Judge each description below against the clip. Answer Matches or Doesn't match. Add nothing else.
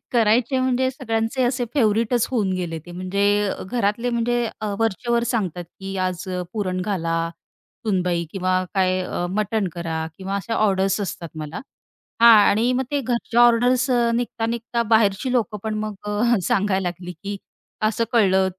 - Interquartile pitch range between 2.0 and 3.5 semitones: Doesn't match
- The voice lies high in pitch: Matches